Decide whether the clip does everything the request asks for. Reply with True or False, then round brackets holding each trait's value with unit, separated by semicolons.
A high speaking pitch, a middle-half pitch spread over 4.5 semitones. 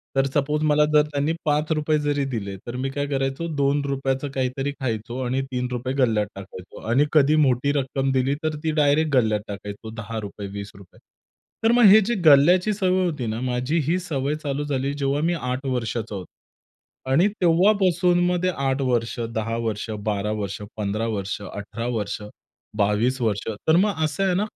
False (135 Hz; 4.9 semitones)